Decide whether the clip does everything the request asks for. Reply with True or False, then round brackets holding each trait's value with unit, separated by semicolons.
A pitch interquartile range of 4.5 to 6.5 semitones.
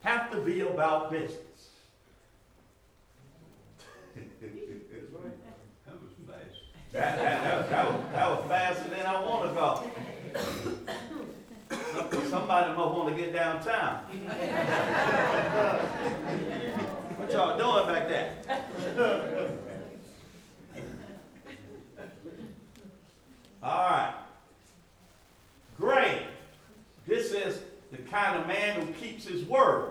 True (4.8 semitones)